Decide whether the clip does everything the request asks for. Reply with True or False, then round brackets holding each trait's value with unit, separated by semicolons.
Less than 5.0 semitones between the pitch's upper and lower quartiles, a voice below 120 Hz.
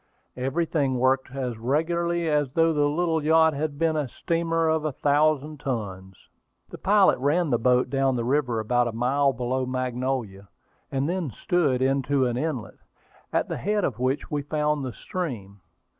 False (3.9 semitones; 140 Hz)